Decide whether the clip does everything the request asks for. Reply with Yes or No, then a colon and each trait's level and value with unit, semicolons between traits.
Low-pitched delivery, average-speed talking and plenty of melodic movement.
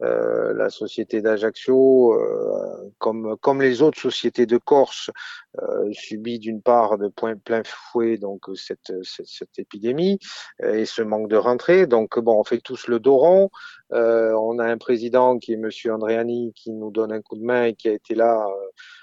Yes: low, 120 Hz; average, 185 wpm; wide, 5.8 semitones